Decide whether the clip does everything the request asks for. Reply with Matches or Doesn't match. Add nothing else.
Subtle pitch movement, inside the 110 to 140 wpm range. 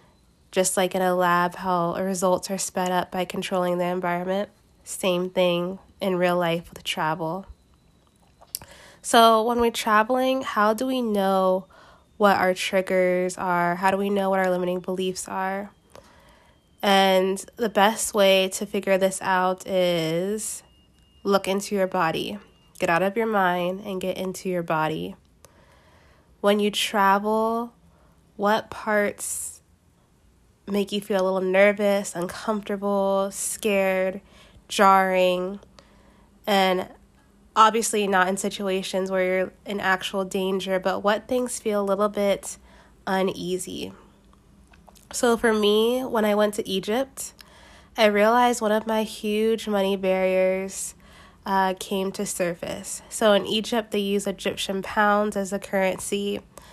Matches